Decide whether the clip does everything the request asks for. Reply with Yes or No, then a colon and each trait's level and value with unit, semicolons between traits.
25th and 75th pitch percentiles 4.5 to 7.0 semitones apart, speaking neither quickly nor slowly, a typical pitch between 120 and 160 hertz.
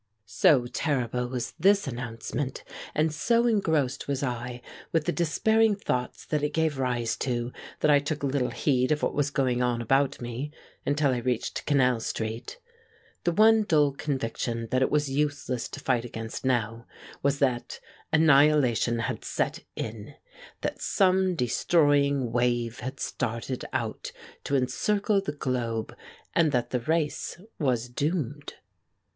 No: average, 3.9 semitones; average, 145 wpm; low, 135 Hz